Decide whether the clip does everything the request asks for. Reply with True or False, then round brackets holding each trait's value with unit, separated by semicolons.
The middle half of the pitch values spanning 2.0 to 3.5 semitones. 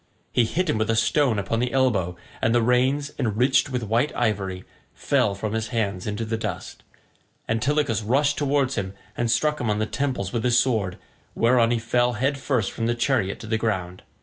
True (3.2 semitones)